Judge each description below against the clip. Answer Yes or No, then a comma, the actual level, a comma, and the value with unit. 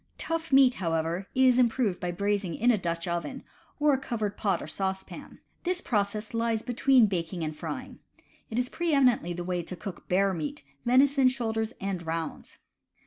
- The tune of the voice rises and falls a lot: Yes, wide, 6.2 semitones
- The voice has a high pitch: Yes, high, 210 Hz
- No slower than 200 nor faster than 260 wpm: No, average, 175 wpm